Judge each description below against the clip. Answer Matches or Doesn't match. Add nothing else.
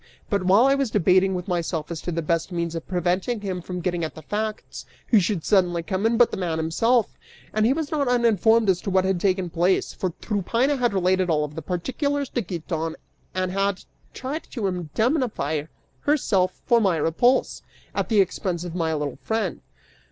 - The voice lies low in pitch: Doesn't match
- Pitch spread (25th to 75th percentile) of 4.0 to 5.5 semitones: Matches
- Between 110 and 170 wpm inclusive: Doesn't match